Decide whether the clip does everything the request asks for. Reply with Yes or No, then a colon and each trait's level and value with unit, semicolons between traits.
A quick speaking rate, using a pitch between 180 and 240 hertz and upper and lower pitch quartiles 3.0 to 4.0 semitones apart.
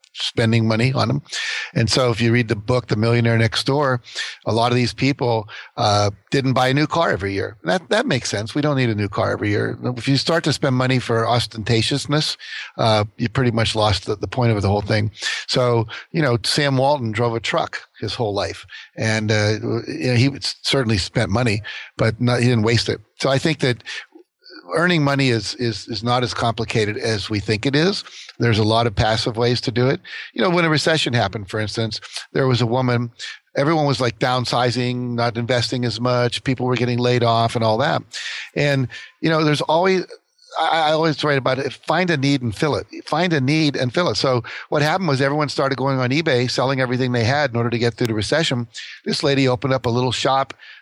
No: fast, 220 wpm; low, 125 Hz; average, 3.4 semitones